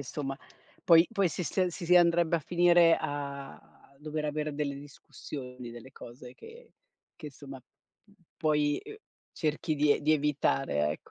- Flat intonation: No, average, 3.4 semitones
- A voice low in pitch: No, medium, 150 Hz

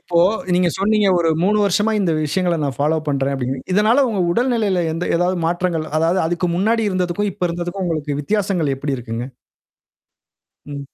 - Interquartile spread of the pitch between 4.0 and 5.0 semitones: Yes, average, 4.7 semitones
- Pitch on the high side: No, medium, 175 Hz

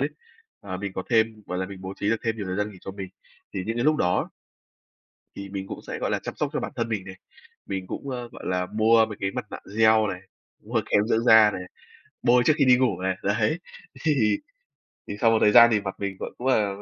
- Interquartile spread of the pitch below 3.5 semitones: Yes, average, 3.1 semitones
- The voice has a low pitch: Yes, low, 105 Hz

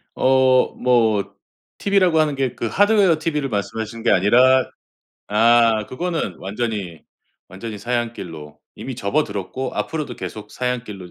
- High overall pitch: No, low, 120 Hz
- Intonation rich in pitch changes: No, average, 4.4 semitones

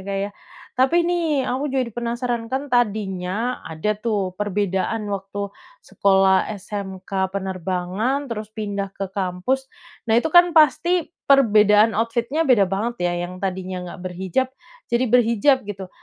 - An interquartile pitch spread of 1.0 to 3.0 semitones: No, average, 4.5 semitones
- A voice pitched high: Yes, high, 210 Hz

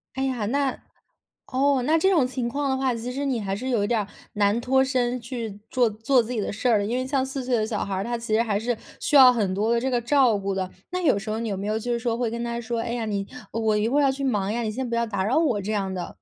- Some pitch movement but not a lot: Yes, average, 3.4 semitones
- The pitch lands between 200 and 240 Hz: Yes, high, 235 Hz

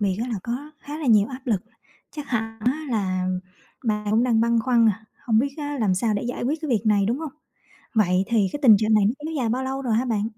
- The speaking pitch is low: No, high, 230 Hz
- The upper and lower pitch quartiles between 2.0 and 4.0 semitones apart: Yes, average, 3.5 semitones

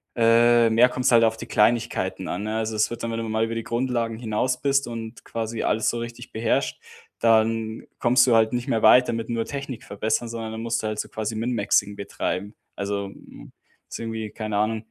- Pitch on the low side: Yes, low, 115 Hz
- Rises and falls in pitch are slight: Yes, narrow, 1.2 semitones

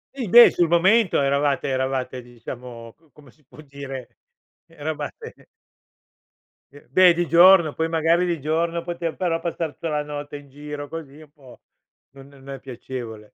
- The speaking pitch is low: No, medium, 150 Hz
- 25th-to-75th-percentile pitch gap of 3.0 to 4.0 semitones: Yes, average, 3.7 semitones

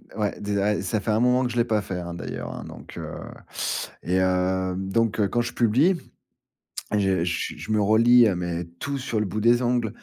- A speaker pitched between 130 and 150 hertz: No, low, 105 Hz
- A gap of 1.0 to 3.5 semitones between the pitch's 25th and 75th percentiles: No, average, 4.2 semitones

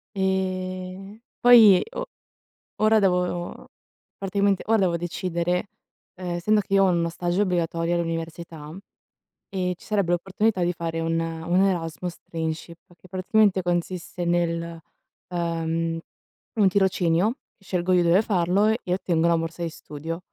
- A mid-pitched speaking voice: Yes, medium, 180 Hz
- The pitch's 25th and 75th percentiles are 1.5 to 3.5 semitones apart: Yes, narrow, 2.4 semitones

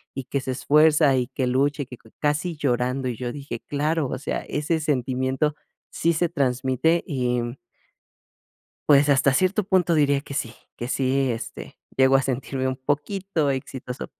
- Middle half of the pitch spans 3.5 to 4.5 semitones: No, average, 2.7 semitones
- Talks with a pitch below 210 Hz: Yes, medium, 140 Hz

